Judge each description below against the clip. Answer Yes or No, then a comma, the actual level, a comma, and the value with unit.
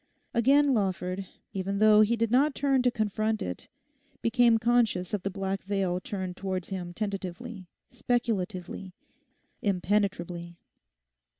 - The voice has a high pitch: Yes, high, 200 Hz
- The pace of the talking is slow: Yes, slow, 120 wpm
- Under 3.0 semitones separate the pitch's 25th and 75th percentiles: No, average, 3.8 semitones